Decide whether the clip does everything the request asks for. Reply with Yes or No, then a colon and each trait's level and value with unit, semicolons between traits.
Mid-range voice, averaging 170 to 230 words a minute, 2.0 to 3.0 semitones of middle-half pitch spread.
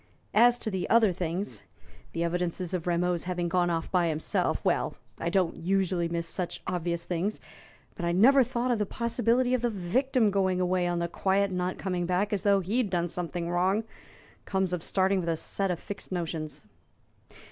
Yes: medium, 180 Hz; average, 190 wpm; average, 2.7 semitones